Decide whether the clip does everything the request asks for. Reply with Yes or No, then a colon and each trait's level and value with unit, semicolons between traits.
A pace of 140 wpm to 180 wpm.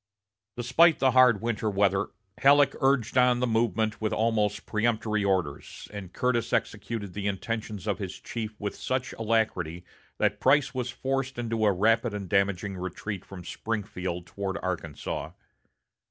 Yes: average, 145 wpm